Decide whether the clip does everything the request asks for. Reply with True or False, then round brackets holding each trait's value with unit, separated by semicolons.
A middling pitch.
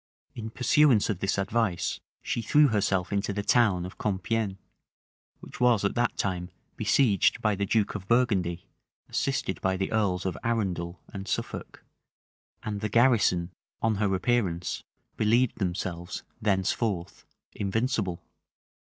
False (100 Hz)